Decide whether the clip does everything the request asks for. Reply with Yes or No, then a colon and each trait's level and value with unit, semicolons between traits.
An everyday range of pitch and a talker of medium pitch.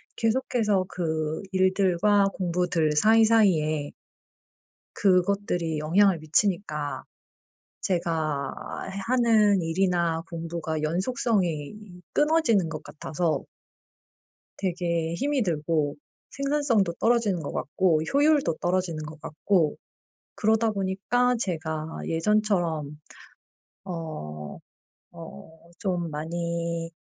Yes: average, 4.5 semitones; medium, 175 Hz